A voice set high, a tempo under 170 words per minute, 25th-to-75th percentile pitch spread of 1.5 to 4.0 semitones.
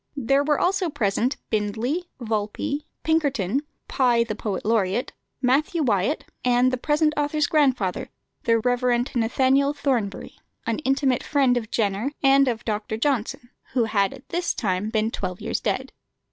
No: high, 245 Hz; average, 145 wpm; average, 4.4 semitones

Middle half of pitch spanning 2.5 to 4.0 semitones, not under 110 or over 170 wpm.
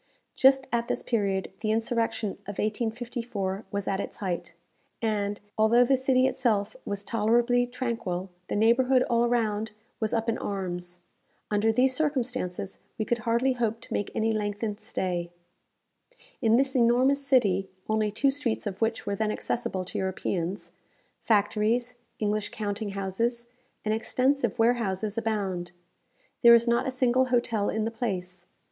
Yes: average, 3.1 semitones; average, 150 wpm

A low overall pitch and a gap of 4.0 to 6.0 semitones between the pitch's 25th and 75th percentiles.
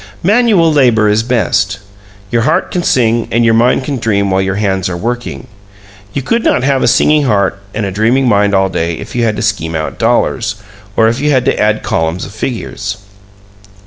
Yes: low, 110 Hz; average, 4.3 semitones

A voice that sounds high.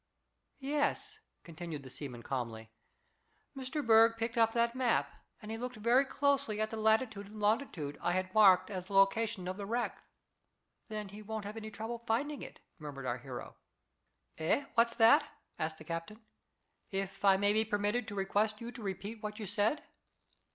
Yes: high, 215 Hz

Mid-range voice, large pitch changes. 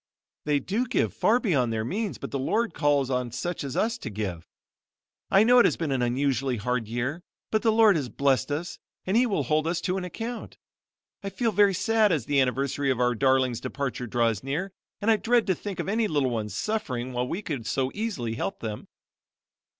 Yes: medium, 145 Hz; wide, 8.6 semitones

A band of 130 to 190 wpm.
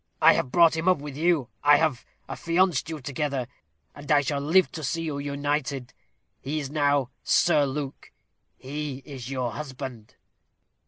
Yes: average, 160 wpm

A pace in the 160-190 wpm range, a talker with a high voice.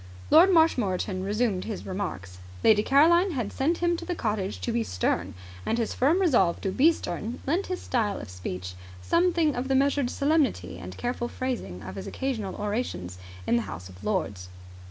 Yes: average, 180 wpm; high, 215 Hz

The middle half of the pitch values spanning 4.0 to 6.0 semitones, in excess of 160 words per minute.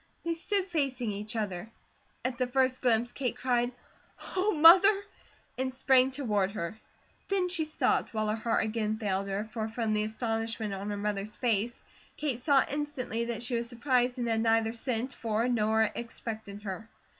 No: average, 3.2 semitones; average, 170 wpm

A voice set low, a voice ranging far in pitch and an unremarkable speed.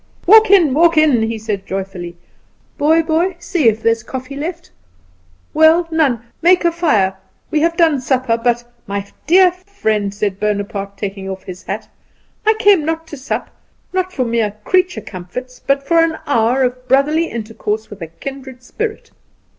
No: very high, 260 Hz; wide, 7.5 semitones; average, 175 wpm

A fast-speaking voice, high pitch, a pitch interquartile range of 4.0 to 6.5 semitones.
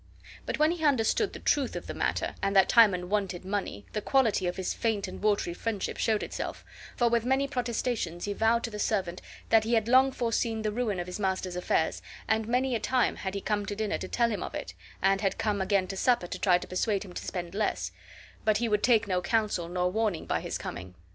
No: fast, 235 wpm; high, 210 Hz; average, 3.6 semitones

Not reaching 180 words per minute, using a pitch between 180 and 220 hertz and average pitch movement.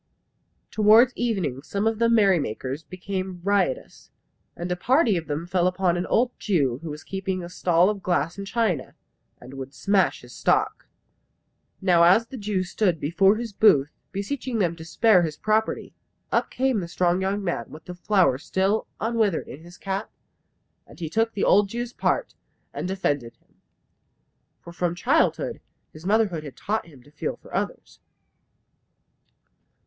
Yes: average, 165 wpm; medium, 185 Hz; average, 4.1 semitones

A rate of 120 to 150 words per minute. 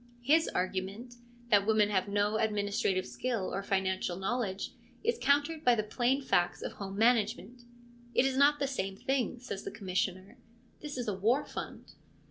No: average, 175 wpm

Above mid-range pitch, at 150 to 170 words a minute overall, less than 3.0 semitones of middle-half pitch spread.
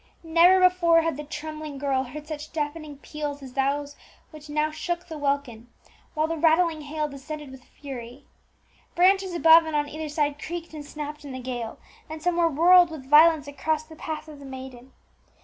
No: very high, 300 Hz; average, 185 wpm; narrow, 2.4 semitones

